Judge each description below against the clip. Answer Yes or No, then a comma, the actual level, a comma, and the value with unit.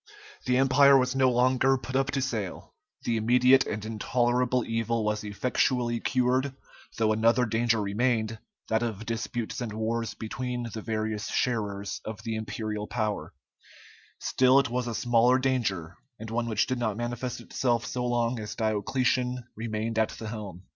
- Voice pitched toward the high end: No, low, 115 Hz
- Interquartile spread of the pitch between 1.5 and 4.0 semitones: Yes, narrow, 2.5 semitones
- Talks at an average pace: Yes, average, 160 wpm